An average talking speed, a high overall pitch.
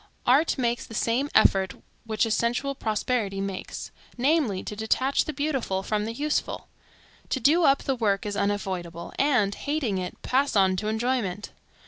Yes: average, 160 wpm; high, 225 Hz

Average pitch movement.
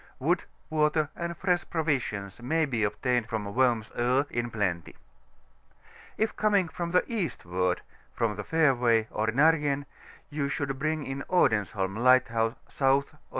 No: wide, 5.8 semitones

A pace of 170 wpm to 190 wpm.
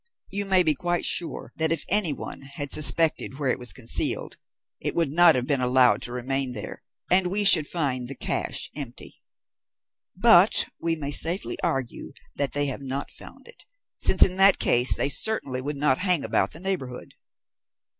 Yes: average, 175 wpm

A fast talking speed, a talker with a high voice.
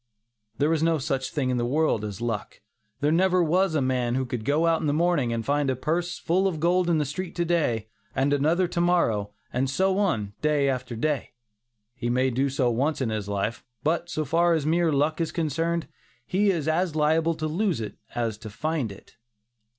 No: fast, 215 wpm; medium, 150 Hz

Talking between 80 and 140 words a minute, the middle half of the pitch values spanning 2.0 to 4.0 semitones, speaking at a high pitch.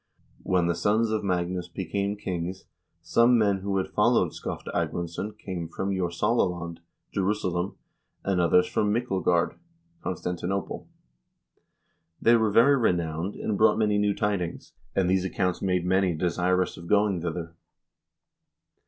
No: slow, 135 wpm; average, 2.9 semitones; very low, 95 Hz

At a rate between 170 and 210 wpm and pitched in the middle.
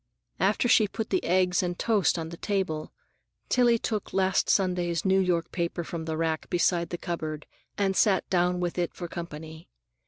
Yes: average, 180 wpm; medium, 175 Hz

